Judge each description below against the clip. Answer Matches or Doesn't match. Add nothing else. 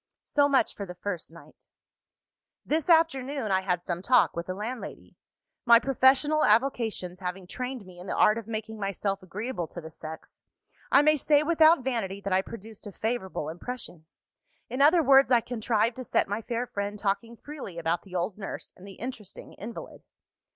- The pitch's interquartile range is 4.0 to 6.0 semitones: Matches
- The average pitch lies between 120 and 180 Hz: Doesn't match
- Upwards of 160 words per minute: Matches